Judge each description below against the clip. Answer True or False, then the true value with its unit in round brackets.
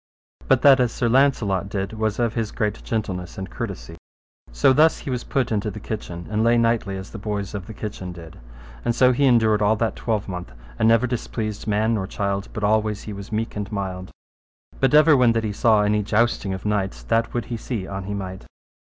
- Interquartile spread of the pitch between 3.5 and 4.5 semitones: False (2.8 semitones)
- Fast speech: True (215 wpm)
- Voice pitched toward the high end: False (105 Hz)